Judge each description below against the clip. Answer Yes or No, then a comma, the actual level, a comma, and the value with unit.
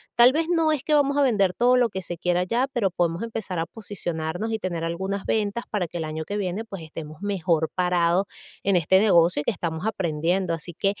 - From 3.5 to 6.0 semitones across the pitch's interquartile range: Yes, average, 4.7 semitones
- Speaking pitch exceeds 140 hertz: Yes, high, 190 Hz